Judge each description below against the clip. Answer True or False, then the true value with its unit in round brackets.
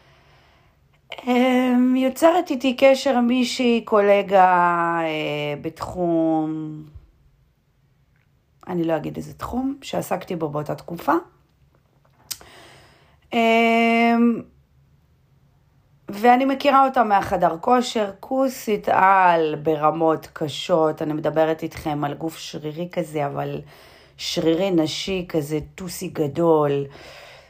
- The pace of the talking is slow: True (85 wpm)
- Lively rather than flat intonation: True (7.2 semitones)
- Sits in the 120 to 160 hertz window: False (170 Hz)